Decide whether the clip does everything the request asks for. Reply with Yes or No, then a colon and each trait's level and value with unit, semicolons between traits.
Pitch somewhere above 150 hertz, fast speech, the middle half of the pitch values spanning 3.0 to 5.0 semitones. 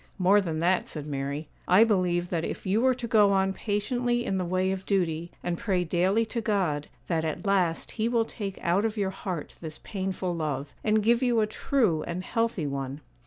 Yes: high, 190 Hz; fast, 210 wpm; average, 4.3 semitones